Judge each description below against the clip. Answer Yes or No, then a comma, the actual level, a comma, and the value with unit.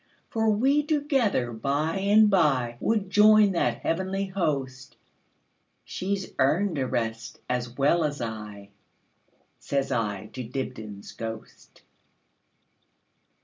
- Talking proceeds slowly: Yes, slow, 100 wpm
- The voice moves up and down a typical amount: No, wide, 8.8 semitones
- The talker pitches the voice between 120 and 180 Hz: Yes, medium, 140 Hz